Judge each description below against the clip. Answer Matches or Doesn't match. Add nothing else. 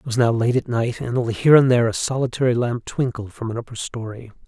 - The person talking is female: Doesn't match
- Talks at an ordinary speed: Doesn't match